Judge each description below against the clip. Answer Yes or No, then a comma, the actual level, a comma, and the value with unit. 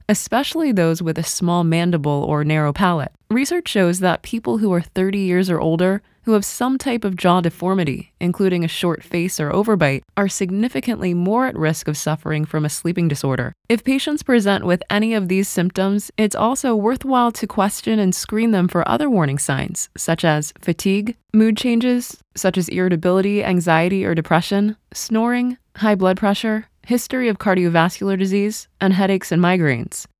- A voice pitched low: No, high, 190 Hz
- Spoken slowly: No, average, 170 wpm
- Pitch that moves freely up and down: No, average, 4.3 semitones